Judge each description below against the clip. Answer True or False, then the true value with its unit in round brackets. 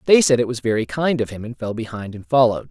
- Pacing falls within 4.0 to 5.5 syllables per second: False (6.7 syllables/s)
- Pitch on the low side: True (120 Hz)